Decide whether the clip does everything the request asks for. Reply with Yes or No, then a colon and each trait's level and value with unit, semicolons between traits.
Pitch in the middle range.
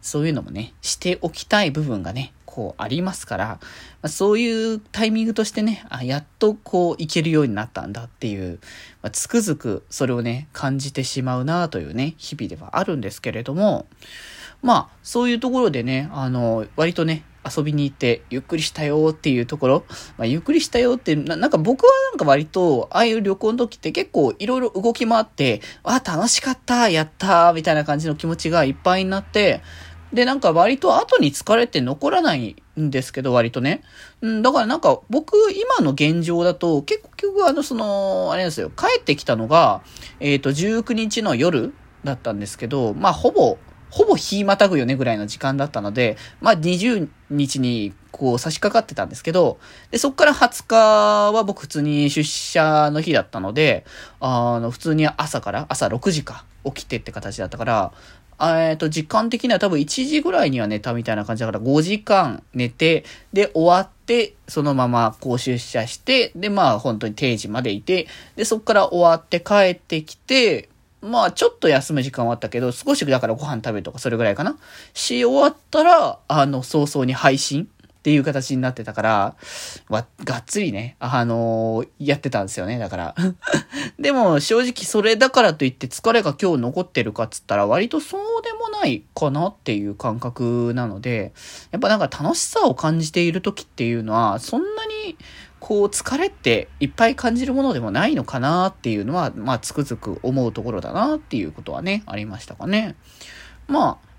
Yes: medium, 155 Hz